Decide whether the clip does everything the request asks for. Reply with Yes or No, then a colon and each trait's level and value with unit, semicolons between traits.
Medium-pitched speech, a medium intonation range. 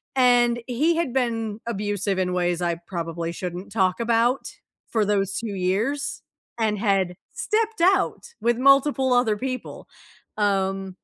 No: high, 220 Hz; average, 5.0 semitones